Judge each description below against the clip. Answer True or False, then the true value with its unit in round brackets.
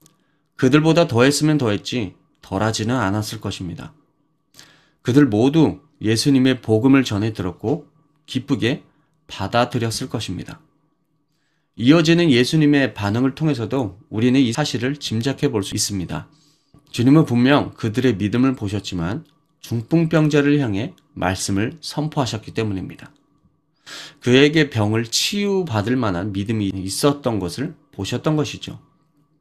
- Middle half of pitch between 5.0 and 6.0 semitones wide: True (5.4 semitones)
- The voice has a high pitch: False (130 Hz)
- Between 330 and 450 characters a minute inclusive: False (290 characters per minute)